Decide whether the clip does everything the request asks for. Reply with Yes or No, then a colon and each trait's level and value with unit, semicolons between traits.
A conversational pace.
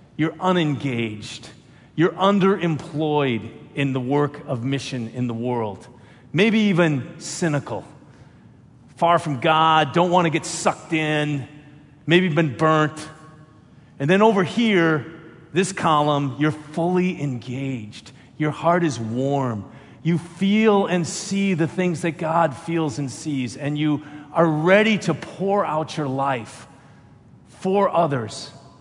No: slow, 130 wpm